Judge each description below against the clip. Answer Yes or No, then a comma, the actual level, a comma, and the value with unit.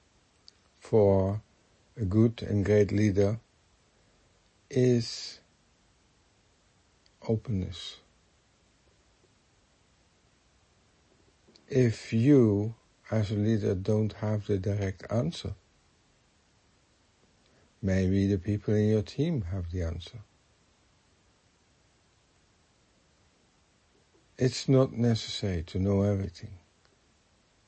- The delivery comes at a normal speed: No, slow, 70 wpm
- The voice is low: Yes, low, 100 Hz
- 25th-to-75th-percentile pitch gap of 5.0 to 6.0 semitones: No, average, 2.7 semitones